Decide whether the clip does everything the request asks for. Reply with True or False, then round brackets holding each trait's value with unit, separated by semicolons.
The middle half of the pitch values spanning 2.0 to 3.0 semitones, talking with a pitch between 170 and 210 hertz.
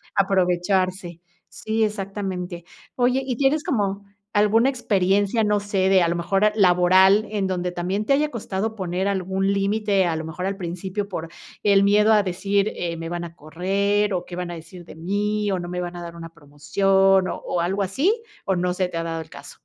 True (2.6 semitones; 190 Hz)